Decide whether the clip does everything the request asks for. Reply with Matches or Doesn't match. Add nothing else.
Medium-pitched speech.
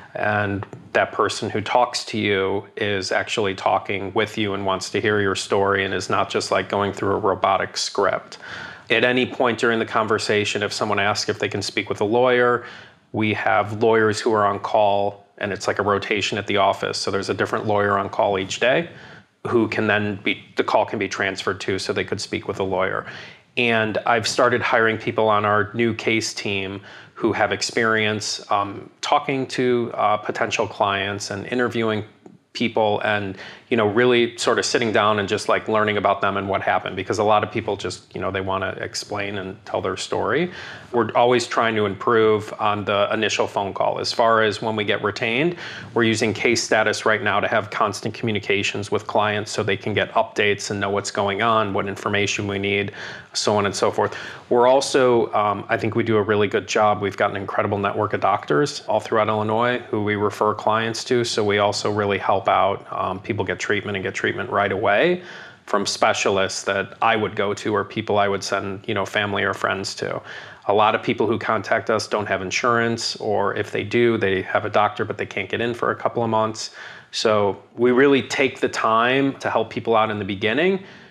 Doesn't match